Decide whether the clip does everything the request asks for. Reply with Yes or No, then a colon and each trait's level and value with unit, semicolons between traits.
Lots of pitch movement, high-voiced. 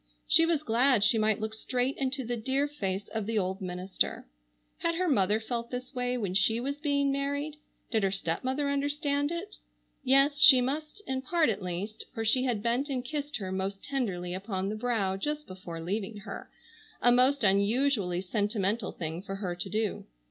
Yes: wide, 6.1 semitones; high, 235 Hz